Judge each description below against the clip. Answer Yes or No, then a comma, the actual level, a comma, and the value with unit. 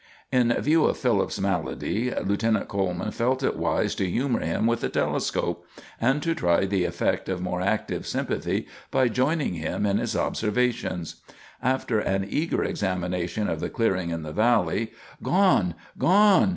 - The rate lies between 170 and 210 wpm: No, average, 155 wpm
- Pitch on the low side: Yes, low, 110 Hz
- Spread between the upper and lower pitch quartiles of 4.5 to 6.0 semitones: Yes, wide, 5.5 semitones